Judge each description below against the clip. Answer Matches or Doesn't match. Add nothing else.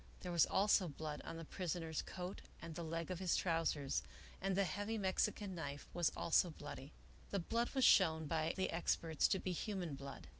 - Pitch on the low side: Doesn't match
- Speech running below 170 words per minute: Doesn't match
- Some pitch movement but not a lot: Matches